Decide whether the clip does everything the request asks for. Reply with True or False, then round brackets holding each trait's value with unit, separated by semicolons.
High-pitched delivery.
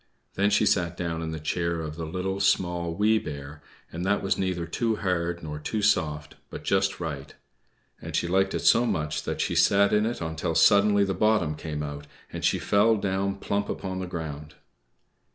False (90 Hz)